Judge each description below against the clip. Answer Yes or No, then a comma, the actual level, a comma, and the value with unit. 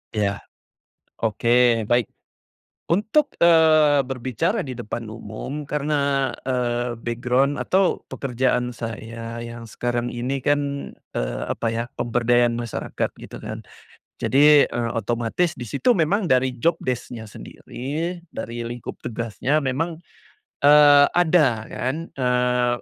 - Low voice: Yes, low, 125 Hz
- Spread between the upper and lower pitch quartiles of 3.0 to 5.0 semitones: Yes, average, 3.7 semitones